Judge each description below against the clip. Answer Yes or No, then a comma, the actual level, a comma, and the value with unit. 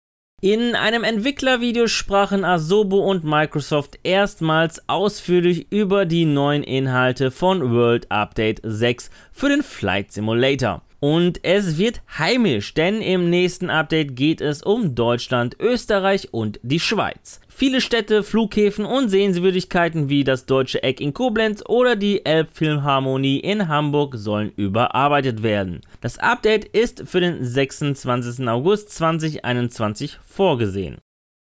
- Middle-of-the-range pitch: Yes, medium, 160 Hz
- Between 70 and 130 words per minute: Yes, slow, 125 wpm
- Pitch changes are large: Yes, wide, 7.6 semitones